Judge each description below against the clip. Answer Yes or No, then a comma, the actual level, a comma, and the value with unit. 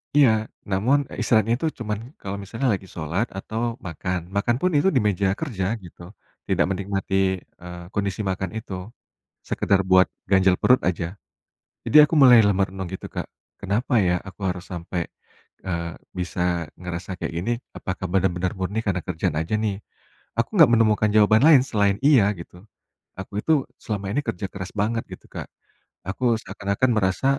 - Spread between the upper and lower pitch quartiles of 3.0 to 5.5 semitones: Yes, average, 3.3 semitones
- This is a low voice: Yes, low, 100 Hz